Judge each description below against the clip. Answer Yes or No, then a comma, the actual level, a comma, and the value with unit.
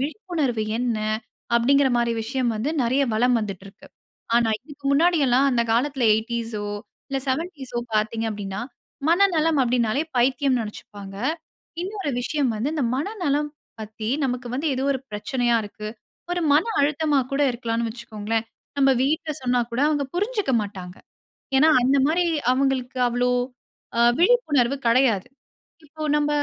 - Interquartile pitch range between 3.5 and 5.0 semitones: Yes, average, 4.2 semitones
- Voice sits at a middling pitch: No, very high, 255 Hz